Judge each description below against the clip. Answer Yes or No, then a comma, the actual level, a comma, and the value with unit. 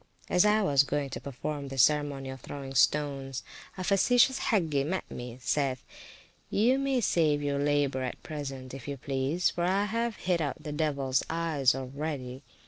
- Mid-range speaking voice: Yes, medium, 145 Hz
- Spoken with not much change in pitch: No, average, 4.3 semitones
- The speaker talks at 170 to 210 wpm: Yes, average, 180 wpm